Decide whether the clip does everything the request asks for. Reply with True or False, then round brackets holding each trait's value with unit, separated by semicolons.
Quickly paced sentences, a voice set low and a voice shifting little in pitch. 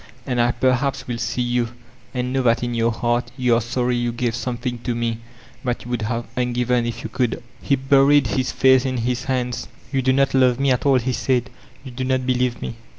True (225 wpm; 125 Hz; 1.5 semitones)